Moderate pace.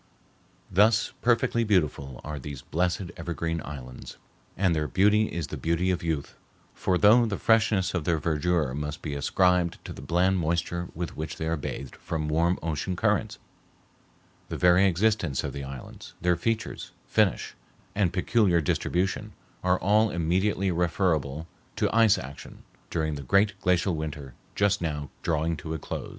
Yes: average, 160 wpm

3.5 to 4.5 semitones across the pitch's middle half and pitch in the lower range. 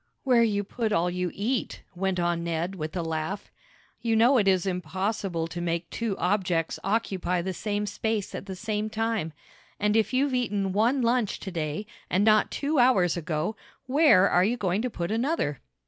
No: average, 4.2 semitones; high, 200 Hz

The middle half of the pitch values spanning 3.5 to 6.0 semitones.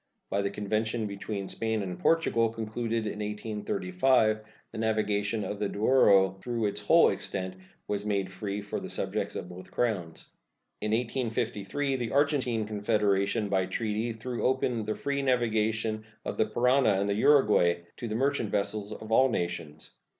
No: narrow, 2.6 semitones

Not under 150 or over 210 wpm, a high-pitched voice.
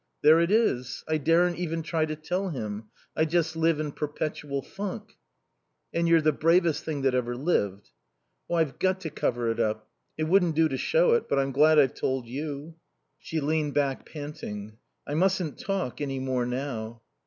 No: average, 185 wpm; medium, 155 Hz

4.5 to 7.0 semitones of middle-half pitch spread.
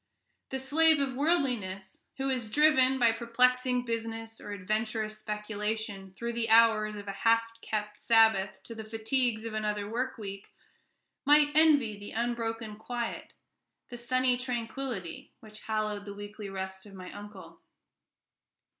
No: average, 3.0 semitones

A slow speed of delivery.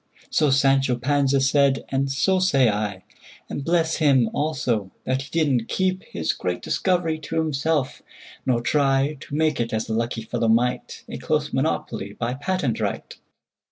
No: average, 145 wpm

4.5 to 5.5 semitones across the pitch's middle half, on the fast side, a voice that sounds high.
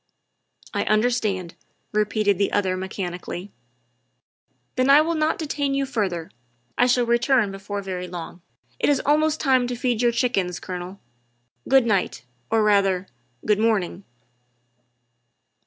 No: average, 5.1 semitones; average, 145 wpm; high, 215 Hz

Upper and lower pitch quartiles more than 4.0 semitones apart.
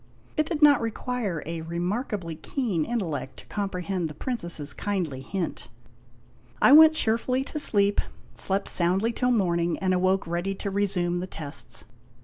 Yes: average, 5.1 semitones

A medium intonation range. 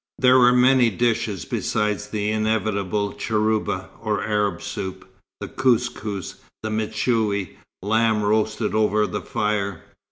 No: narrow, 1.6 semitones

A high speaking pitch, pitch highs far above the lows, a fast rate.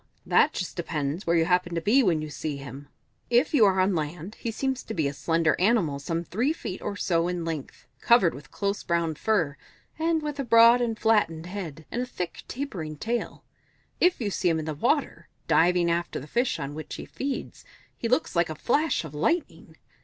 No: medium, 180 Hz; wide, 6.7 semitones; fast, 210 wpm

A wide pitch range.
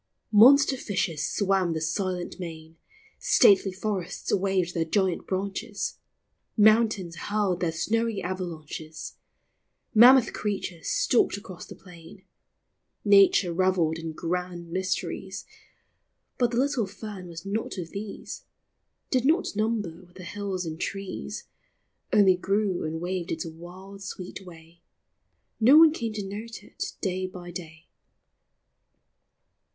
No: average, 3.4 semitones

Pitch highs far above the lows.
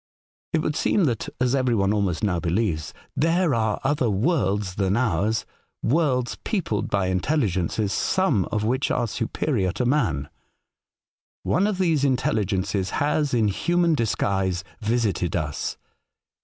Yes: wide, 6.7 semitones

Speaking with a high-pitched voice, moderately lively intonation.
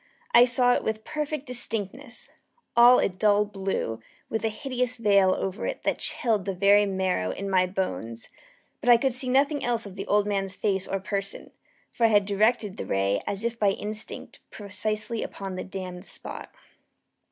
Yes: high, 205 Hz; average, 3.6 semitones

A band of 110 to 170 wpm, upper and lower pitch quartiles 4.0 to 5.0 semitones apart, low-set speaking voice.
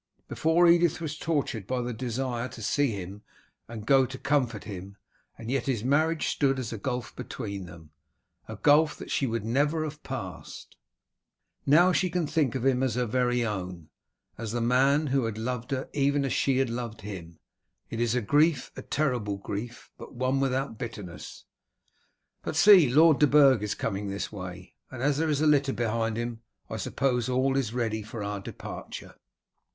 No: average, 185 wpm; average, 4.3 semitones; low, 125 Hz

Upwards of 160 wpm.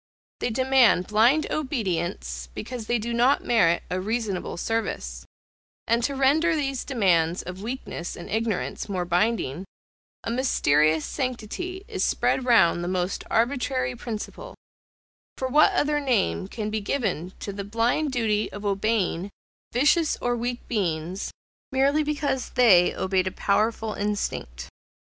No: slow, 135 wpm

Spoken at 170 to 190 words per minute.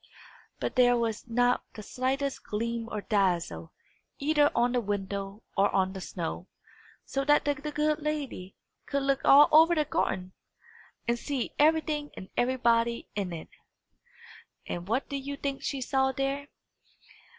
No: average, 150 wpm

